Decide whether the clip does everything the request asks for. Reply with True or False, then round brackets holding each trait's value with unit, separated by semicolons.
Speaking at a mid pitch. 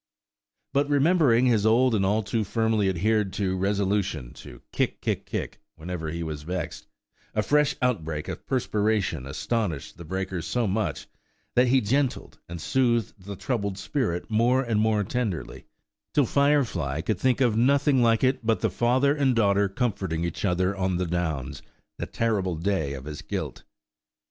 False (105 Hz)